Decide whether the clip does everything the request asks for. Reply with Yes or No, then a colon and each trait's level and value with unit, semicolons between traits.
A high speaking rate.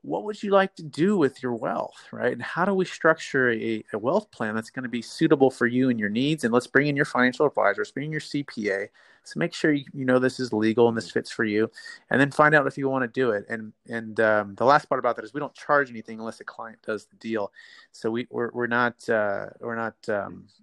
Yes: fast, 270 wpm